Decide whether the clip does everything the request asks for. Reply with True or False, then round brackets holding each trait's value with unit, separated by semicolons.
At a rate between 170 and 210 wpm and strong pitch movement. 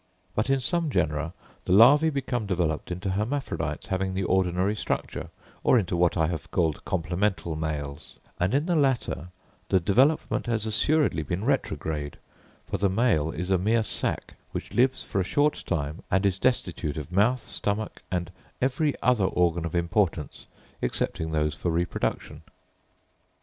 False (155 wpm; 6.4 semitones)